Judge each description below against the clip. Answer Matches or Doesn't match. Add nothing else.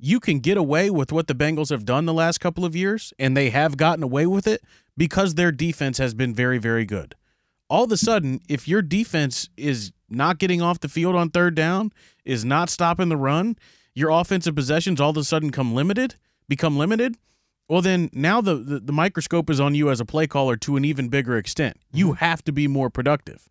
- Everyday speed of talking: Doesn't match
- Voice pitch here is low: Doesn't match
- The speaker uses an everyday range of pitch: Matches